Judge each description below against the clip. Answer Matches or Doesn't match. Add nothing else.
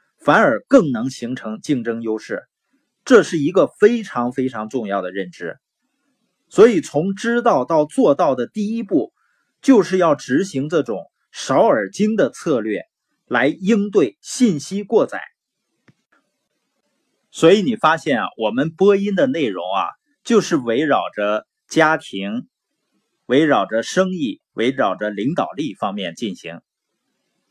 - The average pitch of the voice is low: Doesn't match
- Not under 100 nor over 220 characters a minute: Matches